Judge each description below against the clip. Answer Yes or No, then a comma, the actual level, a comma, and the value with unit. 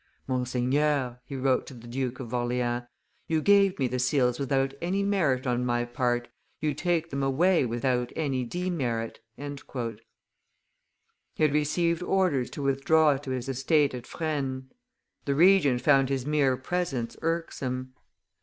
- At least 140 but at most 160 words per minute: Yes, average, 145 wpm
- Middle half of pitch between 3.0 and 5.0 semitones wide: Yes, average, 3.8 semitones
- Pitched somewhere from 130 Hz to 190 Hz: Yes, low, 135 Hz